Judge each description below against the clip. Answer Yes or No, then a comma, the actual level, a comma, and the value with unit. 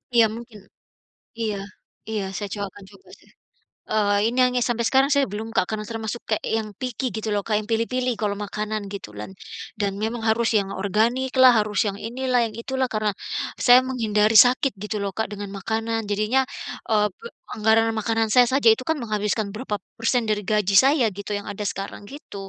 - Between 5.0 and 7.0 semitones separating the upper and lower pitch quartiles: No, average, 2.8 semitones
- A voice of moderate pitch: No, high, 220 Hz